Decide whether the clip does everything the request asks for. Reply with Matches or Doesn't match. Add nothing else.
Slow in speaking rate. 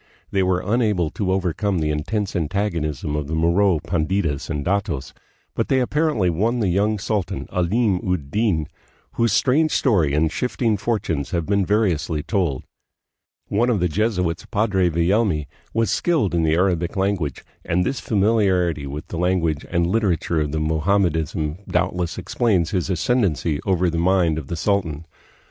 Doesn't match